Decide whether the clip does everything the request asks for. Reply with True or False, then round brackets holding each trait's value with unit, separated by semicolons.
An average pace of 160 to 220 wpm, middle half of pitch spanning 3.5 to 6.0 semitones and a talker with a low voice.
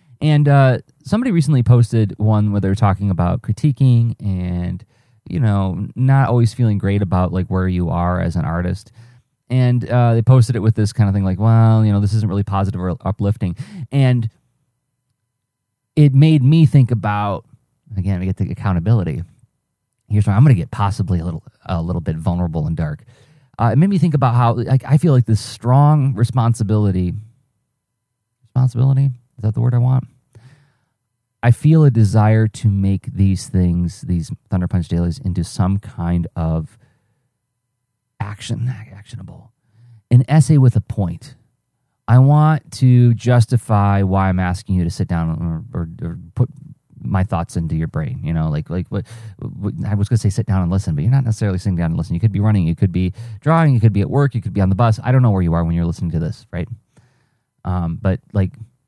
True (195 wpm; 4.8 semitones; 110 Hz)